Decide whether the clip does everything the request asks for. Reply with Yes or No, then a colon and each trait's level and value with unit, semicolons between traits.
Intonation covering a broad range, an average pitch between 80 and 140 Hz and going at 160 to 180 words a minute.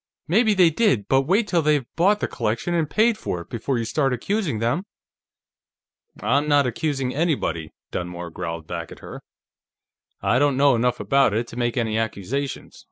Yes: wide, 6.4 semitones; low, 135 Hz; average, 175 wpm